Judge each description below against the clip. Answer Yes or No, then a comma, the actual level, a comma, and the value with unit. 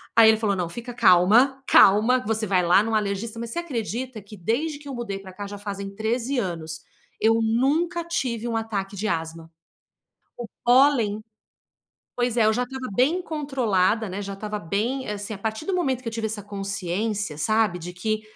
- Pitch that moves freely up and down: No, average, 3.7 semitones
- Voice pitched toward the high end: Yes, high, 220 Hz